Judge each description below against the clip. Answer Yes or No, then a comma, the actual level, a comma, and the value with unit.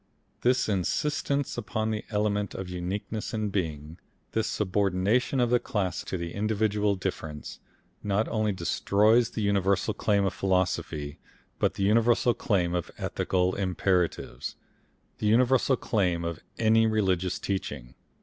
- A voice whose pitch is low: Yes, low, 100 Hz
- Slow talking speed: Yes, slow, 130 wpm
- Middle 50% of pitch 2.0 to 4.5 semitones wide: Yes, average, 3.2 semitones